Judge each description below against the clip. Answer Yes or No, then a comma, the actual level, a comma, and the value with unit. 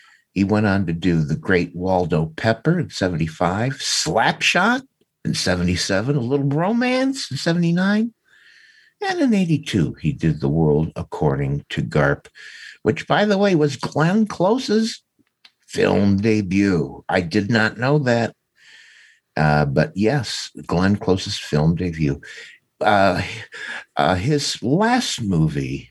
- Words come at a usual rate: No, slow, 125 wpm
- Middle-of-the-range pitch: No, low, 110 Hz